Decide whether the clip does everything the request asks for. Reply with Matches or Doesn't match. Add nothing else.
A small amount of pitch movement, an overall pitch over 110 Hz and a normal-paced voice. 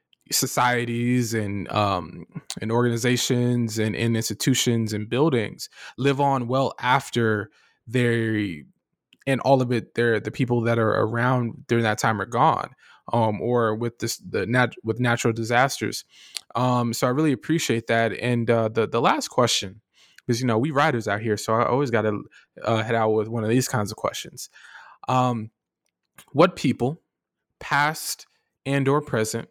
Matches